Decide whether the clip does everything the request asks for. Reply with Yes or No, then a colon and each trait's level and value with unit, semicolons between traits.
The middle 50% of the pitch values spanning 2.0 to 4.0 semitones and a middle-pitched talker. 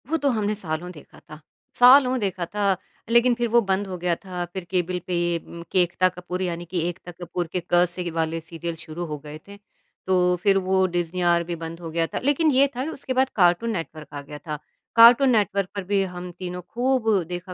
Yes: average, 3.4 semitones; medium, 180 Hz